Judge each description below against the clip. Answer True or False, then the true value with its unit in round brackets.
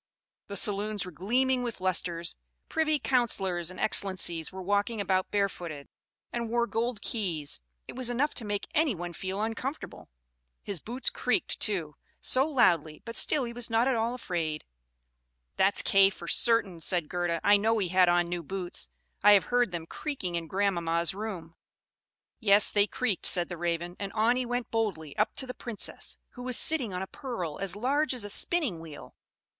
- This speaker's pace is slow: False (180 wpm)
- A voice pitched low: False (200 Hz)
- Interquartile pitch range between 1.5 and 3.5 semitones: False (5.4 semitones)